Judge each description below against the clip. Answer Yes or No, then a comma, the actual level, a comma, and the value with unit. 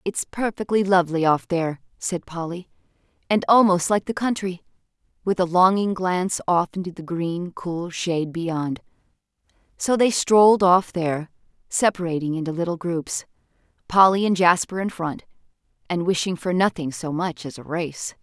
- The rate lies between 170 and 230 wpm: No, average, 150 wpm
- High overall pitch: No, medium, 175 Hz